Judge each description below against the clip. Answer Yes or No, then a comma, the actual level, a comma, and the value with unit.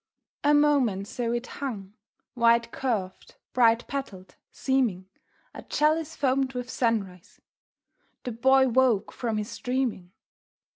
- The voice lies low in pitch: No, high, 245 Hz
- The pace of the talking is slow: Yes, slow, 115 wpm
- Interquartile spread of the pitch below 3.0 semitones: No, average, 3.9 semitones